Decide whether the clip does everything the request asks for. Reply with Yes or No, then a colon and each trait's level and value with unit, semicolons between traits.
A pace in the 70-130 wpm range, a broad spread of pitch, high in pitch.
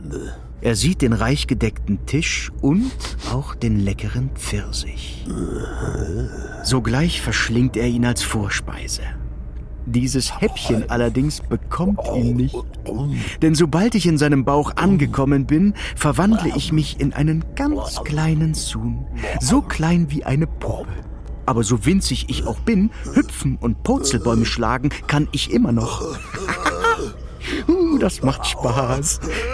No: slow, 125 wpm; wide, 5.7 semitones; low, 130 Hz